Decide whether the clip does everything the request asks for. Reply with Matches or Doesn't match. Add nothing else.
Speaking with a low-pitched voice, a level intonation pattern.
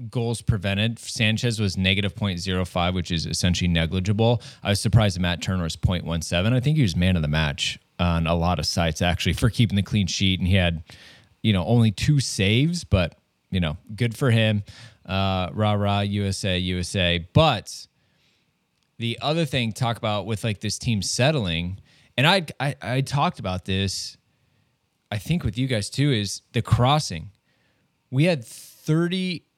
Doesn't match